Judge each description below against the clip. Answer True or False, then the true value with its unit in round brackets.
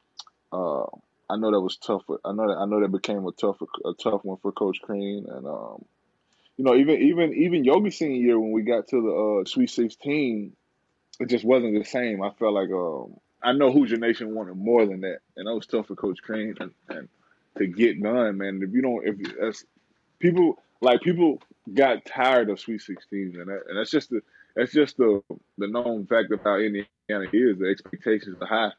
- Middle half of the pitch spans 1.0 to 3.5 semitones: True (3.2 semitones)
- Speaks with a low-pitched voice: True (110 Hz)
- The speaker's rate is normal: False (210 wpm)